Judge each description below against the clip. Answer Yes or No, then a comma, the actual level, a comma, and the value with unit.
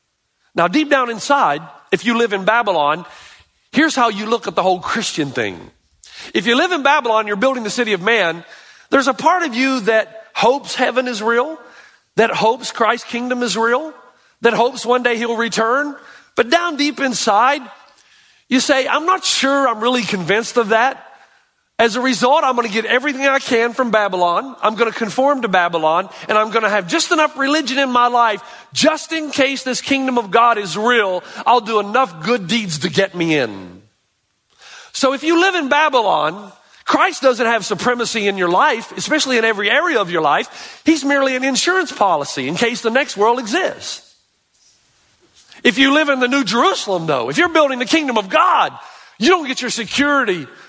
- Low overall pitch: No, high, 245 Hz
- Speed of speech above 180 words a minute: Yes, average, 190 wpm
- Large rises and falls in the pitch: No, average, 4.2 semitones